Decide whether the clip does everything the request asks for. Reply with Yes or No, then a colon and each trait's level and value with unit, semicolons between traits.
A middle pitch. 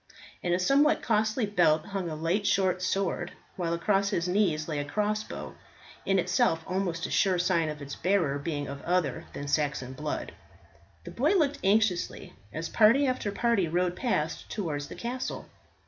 Yes: medium, 180 Hz